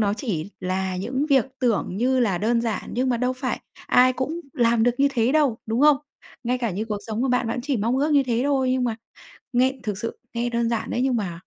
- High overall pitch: Yes, high, 240 Hz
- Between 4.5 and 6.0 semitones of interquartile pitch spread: No, average, 2.8 semitones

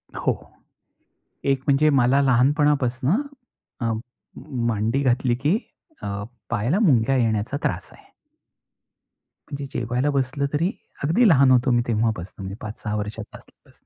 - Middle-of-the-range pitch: No, low, 130 Hz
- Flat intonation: No, average, 3.8 semitones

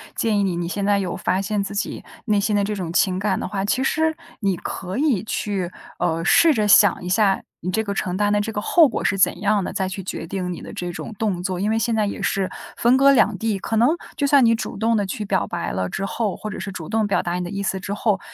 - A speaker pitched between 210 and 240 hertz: No, high, 200 Hz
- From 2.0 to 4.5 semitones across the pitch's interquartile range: Yes, average, 2.8 semitones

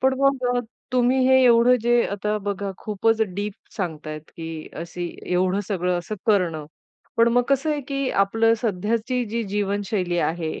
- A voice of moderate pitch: No, high, 210 Hz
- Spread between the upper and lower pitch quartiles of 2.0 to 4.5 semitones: No, average, 5.0 semitones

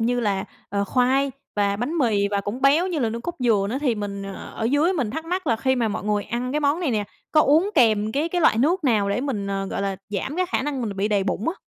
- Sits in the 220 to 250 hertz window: Yes, high, 245 Hz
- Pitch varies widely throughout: Yes, wide, 6.0 semitones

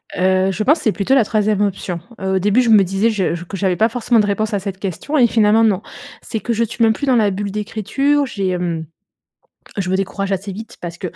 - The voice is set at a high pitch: Yes, high, 205 Hz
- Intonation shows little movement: No, average, 3.0 semitones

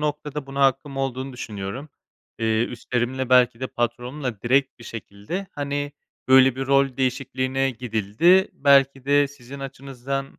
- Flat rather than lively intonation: Yes, narrow, 2.2 semitones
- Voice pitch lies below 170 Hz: Yes, low, 135 Hz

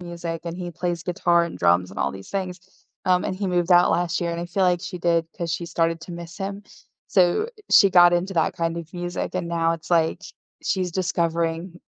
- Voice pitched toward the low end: No, medium, 175 Hz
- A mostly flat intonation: Yes, narrow, 1.3 semitones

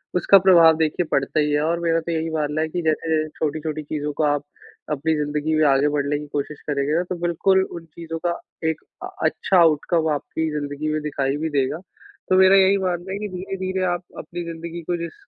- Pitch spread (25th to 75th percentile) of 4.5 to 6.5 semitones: No, average, 2.7 semitones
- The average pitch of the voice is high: No, medium, 160 Hz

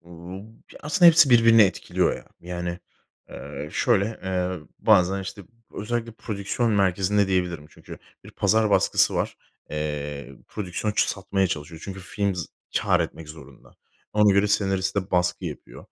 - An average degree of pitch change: Yes, average, 3.1 semitones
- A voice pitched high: No, very low, 95 Hz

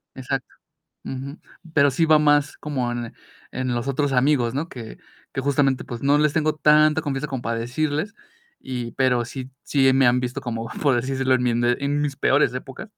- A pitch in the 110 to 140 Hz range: Yes, low, 135 Hz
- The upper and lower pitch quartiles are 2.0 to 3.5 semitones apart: Yes, average, 2.9 semitones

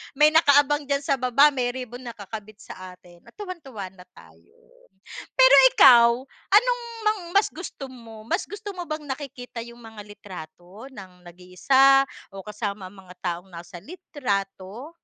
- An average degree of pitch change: No, wide, 6.7 semitones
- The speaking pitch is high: Yes, high, 240 Hz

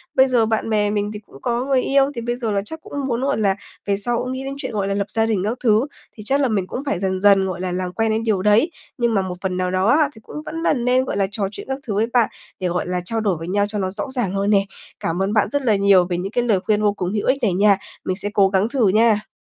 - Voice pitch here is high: Yes, high, 210 Hz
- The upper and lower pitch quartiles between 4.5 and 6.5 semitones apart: No, average, 3.7 semitones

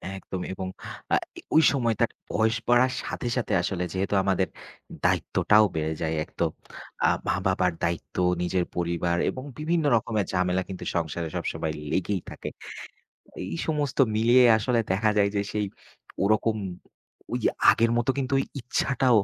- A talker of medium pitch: No, low, 105 Hz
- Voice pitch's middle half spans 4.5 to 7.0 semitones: Yes, average, 4.8 semitones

